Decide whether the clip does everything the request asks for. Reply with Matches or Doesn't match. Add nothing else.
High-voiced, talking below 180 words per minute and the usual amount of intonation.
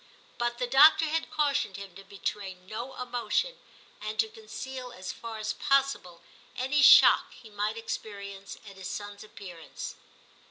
Matches